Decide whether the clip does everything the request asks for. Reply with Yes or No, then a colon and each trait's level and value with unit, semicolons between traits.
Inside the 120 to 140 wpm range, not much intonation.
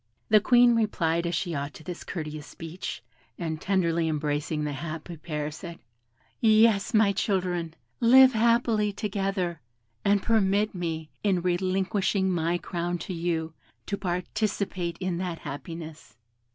No: slow, 135 wpm; average, 3.7 semitones